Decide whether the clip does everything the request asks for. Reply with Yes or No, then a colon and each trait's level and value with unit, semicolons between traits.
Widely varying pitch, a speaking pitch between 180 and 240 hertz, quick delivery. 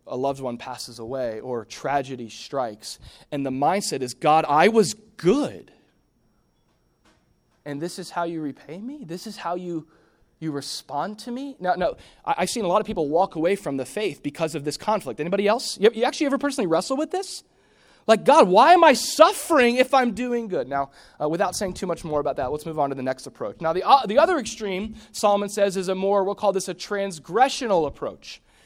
Yes: wide, 7.7 semitones; high, 190 Hz; fast, 215 wpm